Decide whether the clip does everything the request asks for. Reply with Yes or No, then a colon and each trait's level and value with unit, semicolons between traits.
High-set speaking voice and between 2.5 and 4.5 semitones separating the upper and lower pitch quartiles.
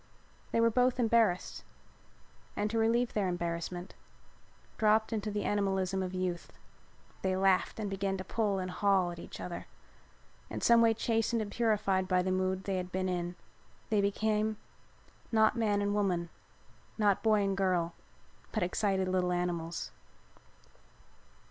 Yes: high, 195 Hz; average, 2.9 semitones